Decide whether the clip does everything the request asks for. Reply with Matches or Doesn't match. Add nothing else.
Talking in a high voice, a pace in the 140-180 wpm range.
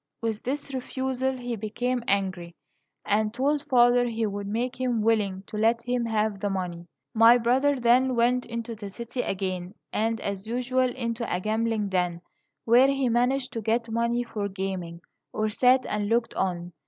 Matches